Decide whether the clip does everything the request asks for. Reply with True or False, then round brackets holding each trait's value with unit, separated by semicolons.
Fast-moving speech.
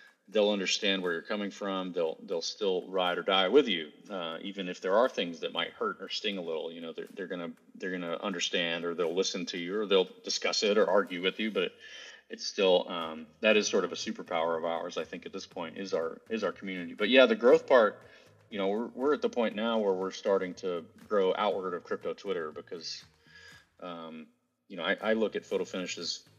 True (235 wpm)